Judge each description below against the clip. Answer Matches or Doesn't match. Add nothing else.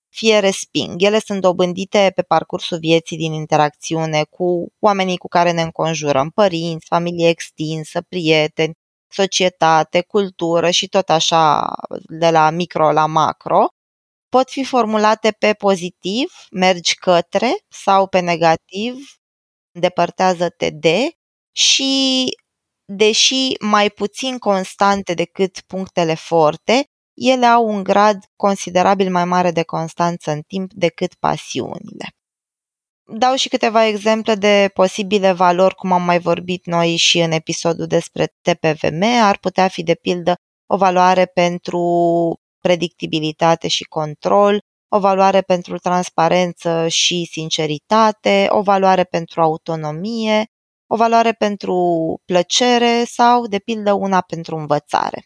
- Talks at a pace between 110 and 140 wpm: Matches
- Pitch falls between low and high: Matches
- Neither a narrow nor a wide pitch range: Matches